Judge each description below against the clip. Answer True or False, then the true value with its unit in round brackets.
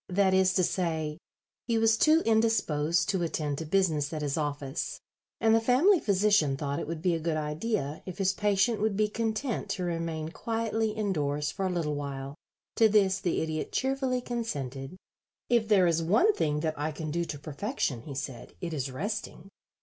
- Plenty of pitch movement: True (6.2 semitones)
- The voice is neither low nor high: True (175 Hz)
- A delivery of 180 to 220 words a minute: True (190 wpm)